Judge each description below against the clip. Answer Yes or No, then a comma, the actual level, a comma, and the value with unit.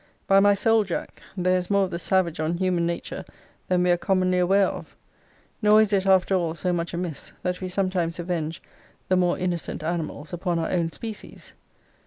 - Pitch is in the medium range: Yes, medium, 180 Hz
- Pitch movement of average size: No, narrow, 1.9 semitones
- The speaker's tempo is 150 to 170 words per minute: No, average, 195 wpm